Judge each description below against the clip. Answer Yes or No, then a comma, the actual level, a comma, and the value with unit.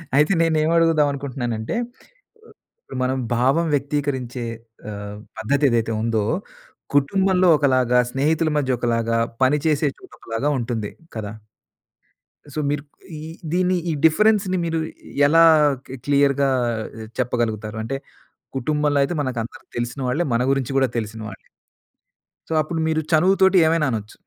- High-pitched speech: No, medium, 140 Hz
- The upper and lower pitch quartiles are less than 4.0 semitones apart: No, average, 5.2 semitones